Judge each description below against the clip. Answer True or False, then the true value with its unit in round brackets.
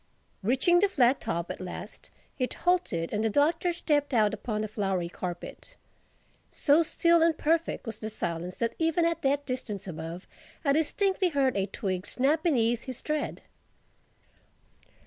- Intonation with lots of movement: True (8.1 semitones)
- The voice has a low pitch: False (255 Hz)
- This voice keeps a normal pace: True (155 wpm)